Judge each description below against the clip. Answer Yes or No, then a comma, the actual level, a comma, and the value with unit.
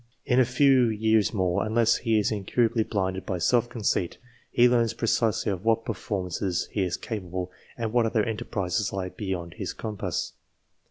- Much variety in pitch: No, average, 3.7 semitones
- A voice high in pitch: No, low, 110 Hz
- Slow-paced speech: No, average, 165 wpm